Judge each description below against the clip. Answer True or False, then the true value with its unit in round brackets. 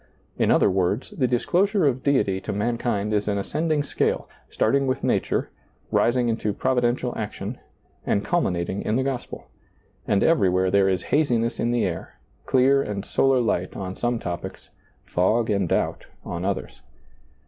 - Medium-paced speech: True (155 wpm)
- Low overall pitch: True (115 Hz)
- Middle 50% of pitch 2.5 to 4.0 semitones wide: False (4.9 semitones)